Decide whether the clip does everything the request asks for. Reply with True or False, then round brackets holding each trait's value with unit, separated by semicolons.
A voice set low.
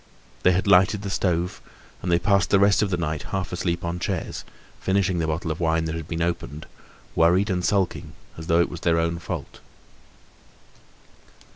True (85 Hz)